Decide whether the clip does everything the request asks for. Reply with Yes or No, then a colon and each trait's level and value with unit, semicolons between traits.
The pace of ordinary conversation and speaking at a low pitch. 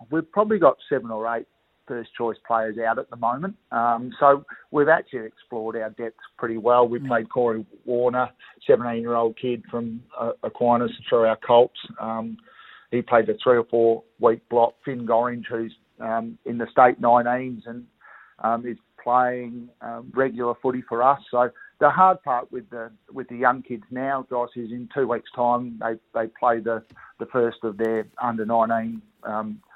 Yes: average, 175 wpm; low, 120 Hz